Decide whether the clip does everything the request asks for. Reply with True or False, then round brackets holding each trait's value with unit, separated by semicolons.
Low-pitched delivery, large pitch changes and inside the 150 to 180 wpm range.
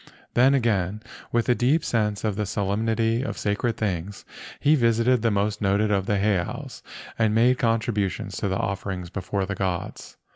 False (105 Hz; 2.8 semitones; 170 wpm)